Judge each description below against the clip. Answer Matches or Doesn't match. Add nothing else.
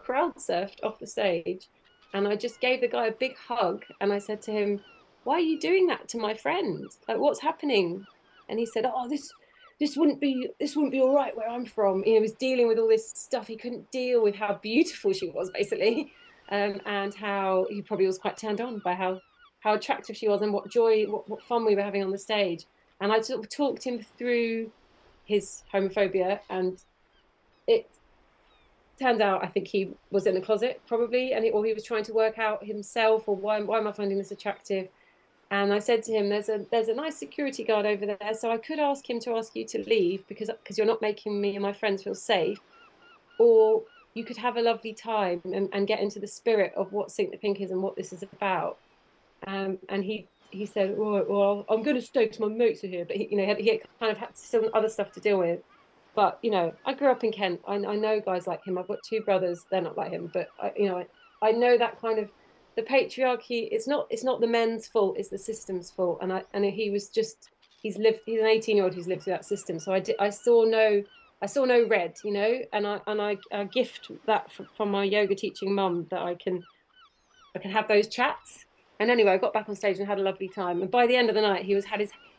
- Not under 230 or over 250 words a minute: Matches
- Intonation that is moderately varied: Matches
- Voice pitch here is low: Doesn't match